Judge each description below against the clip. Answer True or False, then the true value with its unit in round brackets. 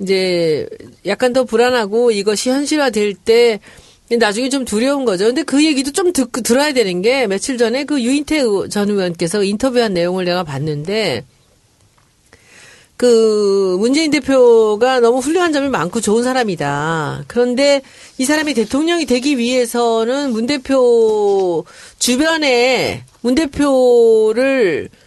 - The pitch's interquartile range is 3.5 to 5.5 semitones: True (5.2 semitones)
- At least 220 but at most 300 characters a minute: True (275 characters per minute)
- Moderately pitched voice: False (240 Hz)